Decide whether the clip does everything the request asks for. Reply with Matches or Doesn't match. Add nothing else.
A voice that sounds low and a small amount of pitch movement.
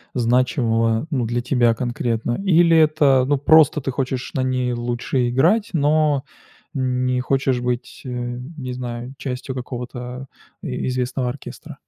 Matches